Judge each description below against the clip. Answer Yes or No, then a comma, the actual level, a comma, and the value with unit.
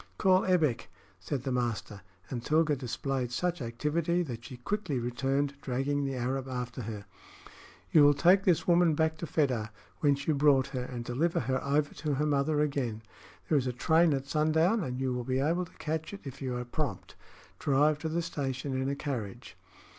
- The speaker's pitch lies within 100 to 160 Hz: Yes, medium, 140 Hz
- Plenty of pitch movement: No, average, 3.9 semitones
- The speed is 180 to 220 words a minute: Yes, average, 190 wpm